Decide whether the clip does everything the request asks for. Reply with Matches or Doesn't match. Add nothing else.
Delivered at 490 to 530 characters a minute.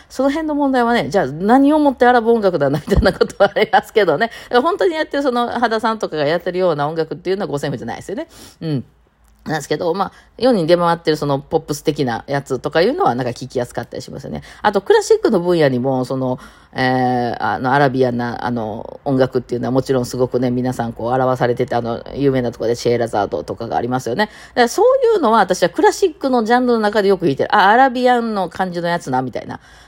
Matches